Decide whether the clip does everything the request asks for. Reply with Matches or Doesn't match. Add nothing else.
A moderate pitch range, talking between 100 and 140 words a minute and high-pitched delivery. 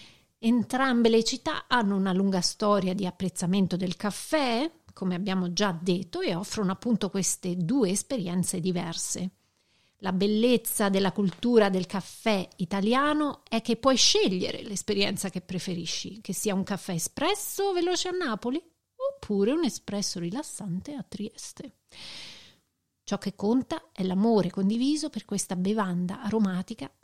Matches